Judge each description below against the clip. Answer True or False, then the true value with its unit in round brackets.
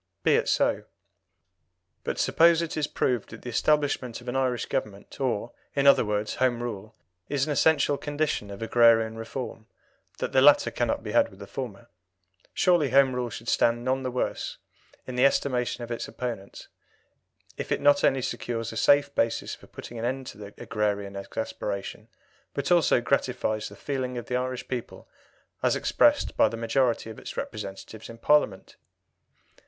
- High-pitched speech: False (125 Hz)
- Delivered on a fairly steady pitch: False (3.4 semitones)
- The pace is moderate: True (175 wpm)